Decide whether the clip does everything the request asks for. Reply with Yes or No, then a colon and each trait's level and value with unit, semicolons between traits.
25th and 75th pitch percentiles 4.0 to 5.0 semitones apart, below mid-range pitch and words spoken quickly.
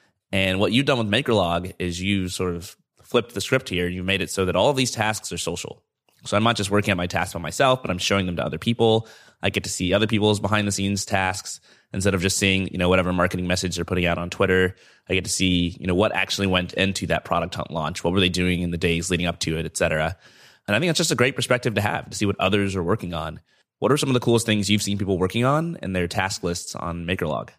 No: average, 3.2 semitones; very low, 95 Hz; fast, 275 wpm